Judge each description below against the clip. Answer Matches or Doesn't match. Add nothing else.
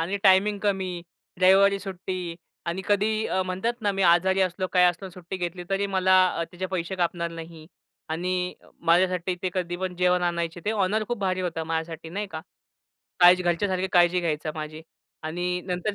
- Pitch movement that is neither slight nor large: Doesn't match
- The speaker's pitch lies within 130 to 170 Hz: Doesn't match